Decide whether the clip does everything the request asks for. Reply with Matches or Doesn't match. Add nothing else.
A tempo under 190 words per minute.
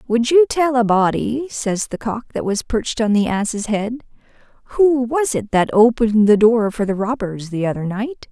Doesn't match